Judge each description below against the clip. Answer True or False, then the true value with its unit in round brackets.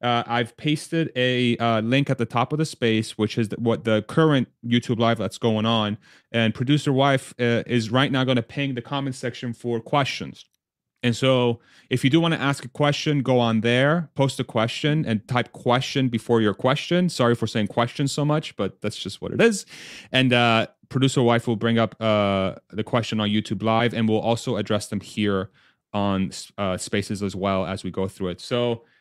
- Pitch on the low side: True (120 Hz)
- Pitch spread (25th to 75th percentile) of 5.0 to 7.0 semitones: False (3.4 semitones)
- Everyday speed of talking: False (210 wpm)